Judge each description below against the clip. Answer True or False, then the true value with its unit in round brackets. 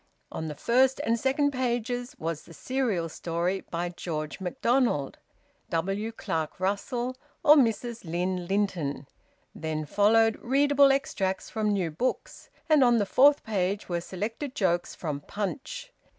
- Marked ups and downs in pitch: True (6.5 semitones)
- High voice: True (205 Hz)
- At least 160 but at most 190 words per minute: False (135 wpm)